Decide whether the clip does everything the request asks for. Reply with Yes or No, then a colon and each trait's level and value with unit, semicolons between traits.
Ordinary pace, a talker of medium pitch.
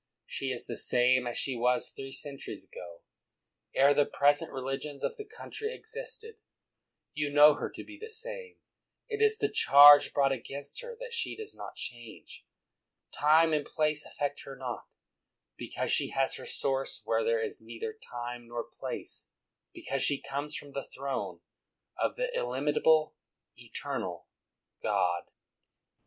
Yes: average, 155 wpm; medium, 145 Hz